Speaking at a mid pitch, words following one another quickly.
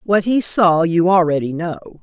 No: medium, 175 Hz; average, 180 wpm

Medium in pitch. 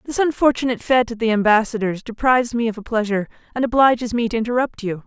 No: high, 230 Hz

